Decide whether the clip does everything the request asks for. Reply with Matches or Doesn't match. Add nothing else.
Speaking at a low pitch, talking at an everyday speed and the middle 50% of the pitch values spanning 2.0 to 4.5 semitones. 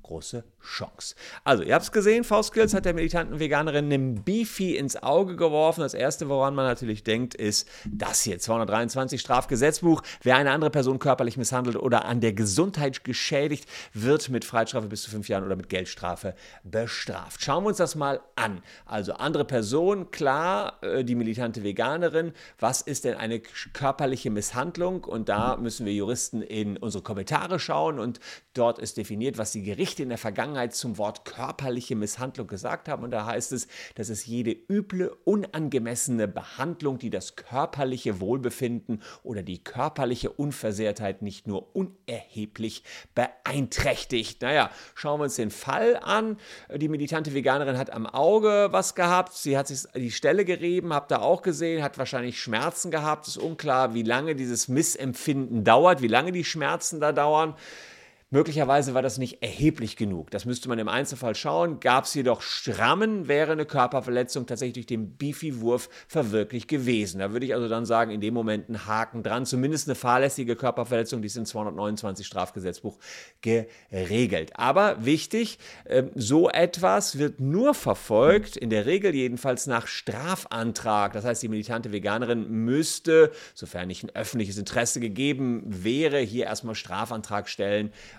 Doesn't match